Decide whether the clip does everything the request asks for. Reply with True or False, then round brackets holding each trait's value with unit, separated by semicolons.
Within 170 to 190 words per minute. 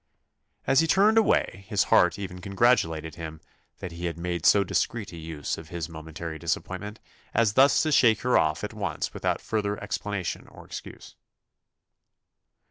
False (160 wpm)